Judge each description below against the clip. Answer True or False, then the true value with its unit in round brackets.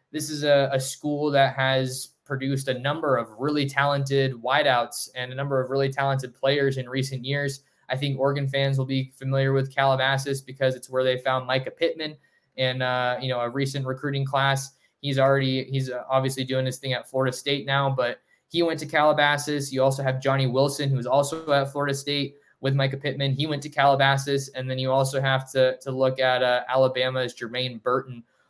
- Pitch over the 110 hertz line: True (135 Hz)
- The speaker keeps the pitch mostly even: True (1.2 semitones)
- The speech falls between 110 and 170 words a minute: False (200 wpm)